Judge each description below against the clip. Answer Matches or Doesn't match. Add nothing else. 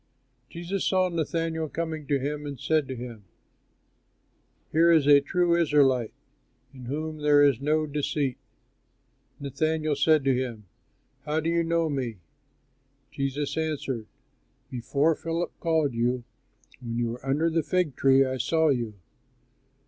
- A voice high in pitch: Doesn't match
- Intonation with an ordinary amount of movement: Matches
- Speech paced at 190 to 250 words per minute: Doesn't match